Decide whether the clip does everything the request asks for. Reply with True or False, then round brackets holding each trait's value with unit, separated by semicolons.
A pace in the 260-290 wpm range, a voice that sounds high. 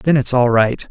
False (265 wpm; 125 Hz)